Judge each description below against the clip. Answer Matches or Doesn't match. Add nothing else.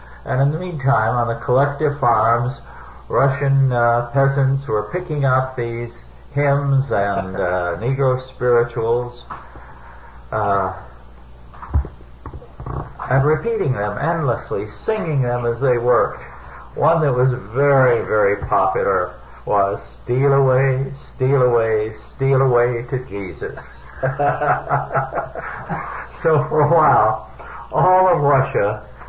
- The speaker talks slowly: Matches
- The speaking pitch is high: Doesn't match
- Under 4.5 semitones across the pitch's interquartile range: Matches